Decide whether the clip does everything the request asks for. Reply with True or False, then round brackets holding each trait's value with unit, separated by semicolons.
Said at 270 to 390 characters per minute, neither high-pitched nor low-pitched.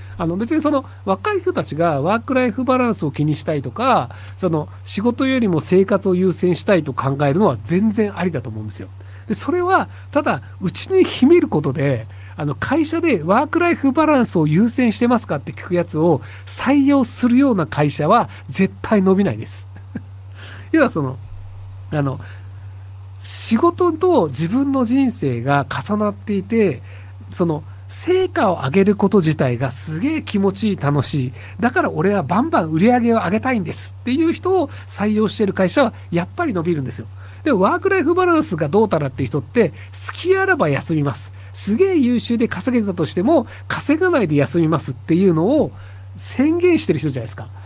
True (365 characters per minute; 175 Hz)